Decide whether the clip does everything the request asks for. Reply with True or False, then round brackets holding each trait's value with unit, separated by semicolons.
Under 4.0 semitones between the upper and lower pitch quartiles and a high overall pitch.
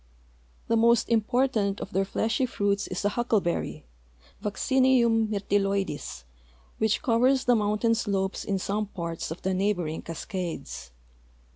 True (3.1 semitones; 205 Hz)